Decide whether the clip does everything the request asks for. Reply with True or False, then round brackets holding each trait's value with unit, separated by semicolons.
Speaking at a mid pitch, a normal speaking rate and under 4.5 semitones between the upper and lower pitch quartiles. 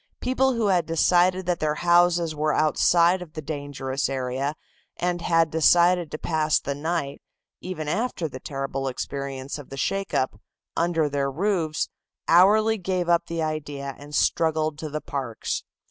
True (160 Hz; 160 wpm; 3.6 semitones)